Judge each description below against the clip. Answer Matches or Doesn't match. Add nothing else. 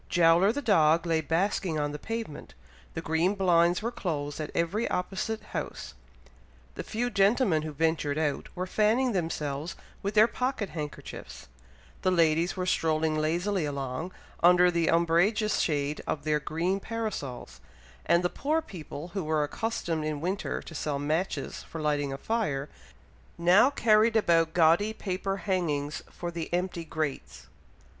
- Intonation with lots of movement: Doesn't match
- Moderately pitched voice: Matches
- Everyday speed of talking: Matches